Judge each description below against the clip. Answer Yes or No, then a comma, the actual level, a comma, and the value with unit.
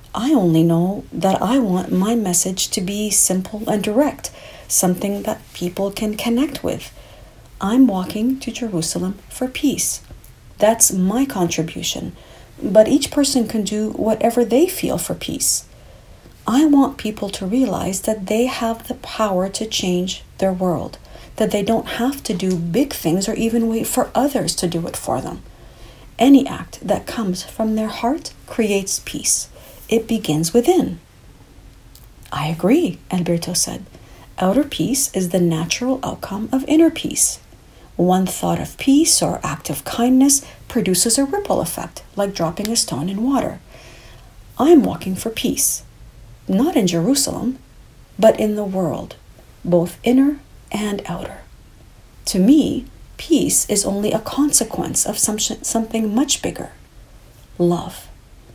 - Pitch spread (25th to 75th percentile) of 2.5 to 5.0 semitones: No, wide, 5.4 semitones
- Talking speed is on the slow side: No, average, 145 wpm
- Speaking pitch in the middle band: No, high, 215 Hz